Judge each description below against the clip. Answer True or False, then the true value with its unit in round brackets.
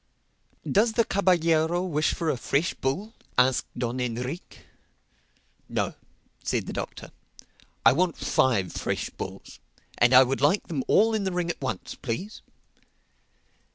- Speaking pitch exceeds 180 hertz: False (155 Hz)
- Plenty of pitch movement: True (6.4 semitones)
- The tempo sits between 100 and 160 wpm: True (140 wpm)